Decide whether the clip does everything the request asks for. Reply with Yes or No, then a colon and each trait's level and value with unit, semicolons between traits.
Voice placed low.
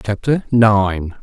Yes: low, 105 Hz